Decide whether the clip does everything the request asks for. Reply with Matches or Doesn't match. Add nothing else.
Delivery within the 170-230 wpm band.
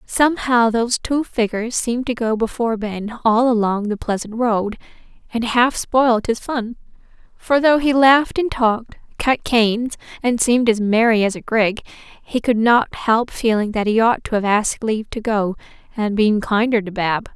Matches